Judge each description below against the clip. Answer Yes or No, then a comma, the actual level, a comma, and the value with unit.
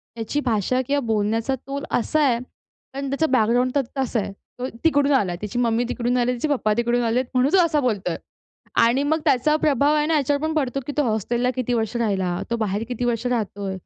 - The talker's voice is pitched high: Yes, high, 245 Hz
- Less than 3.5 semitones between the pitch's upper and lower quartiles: No, average, 3.8 semitones